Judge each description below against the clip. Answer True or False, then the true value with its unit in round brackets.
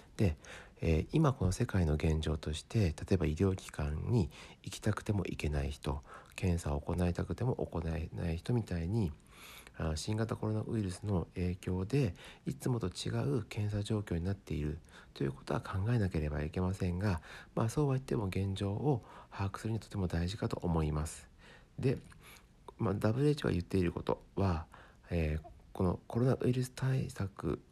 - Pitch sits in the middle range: False (95 Hz)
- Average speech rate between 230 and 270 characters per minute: False (330 characters per minute)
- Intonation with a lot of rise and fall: True (5.7 semitones)